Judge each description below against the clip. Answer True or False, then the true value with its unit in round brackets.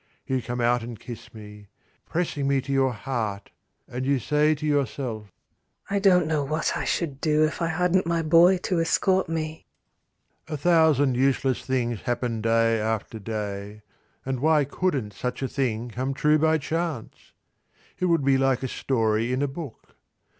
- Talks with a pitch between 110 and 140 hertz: True (135 Hz)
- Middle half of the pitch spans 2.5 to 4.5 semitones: False (4.9 semitones)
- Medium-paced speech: True (170 wpm)